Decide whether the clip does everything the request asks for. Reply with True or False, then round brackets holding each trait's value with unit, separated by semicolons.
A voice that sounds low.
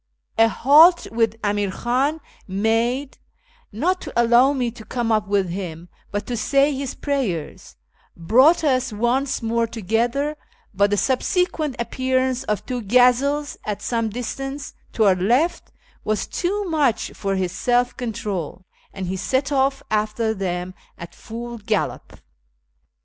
False (235 Hz)